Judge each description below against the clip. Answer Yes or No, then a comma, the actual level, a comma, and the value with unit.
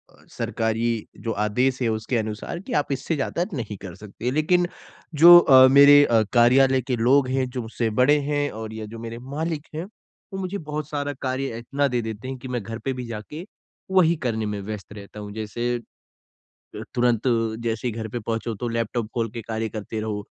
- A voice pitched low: Yes, low, 120 Hz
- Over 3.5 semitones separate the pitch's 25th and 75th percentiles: Yes, average, 4.0 semitones